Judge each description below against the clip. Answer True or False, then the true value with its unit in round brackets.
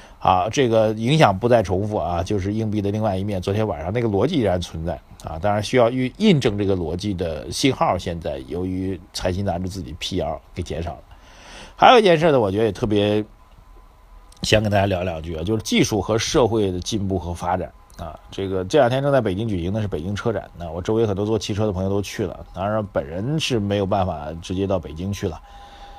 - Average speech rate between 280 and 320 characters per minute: False (335 characters per minute)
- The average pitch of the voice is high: False (100 Hz)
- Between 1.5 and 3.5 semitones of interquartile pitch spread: True (3.1 semitones)